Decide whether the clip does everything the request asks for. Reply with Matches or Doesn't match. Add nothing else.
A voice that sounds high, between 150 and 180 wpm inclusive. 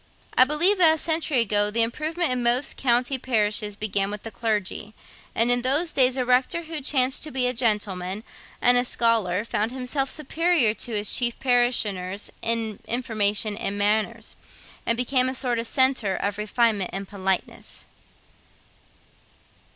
Matches